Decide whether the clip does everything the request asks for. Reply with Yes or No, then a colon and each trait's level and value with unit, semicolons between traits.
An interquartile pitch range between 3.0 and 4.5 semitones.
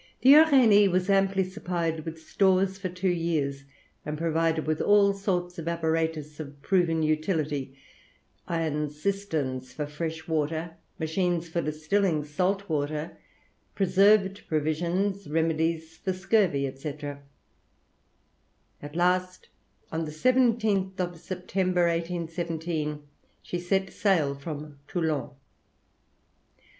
Yes: average, 3.5 semitones